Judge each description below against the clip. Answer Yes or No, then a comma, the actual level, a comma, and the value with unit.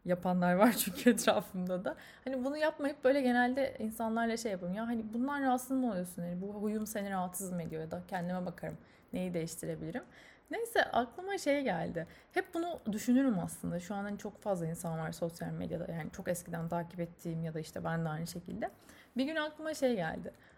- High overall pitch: Yes, high, 205 Hz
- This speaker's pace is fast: Yes, fast, 190 wpm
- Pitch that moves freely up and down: Yes, wide, 6.4 semitones